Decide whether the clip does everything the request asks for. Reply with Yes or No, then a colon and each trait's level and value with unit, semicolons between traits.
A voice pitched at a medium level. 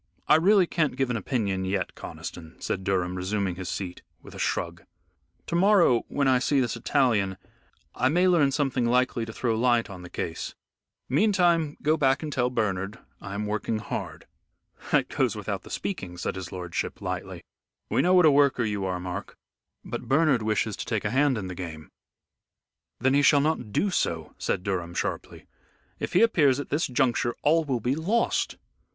No: low, 120 Hz